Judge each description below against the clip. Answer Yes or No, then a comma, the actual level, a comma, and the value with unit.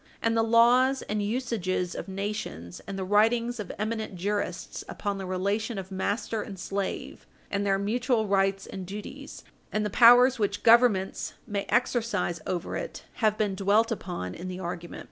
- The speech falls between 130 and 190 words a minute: Yes, average, 165 wpm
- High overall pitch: Yes, high, 205 Hz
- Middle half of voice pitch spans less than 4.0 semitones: Yes, average, 3.0 semitones